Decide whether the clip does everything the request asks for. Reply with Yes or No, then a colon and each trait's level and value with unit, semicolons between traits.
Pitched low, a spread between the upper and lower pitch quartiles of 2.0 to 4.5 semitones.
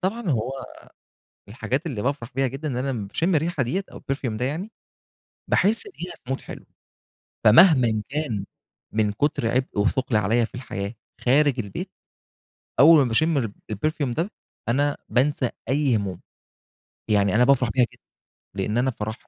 No: low, 130 Hz; average, 5.1 semitones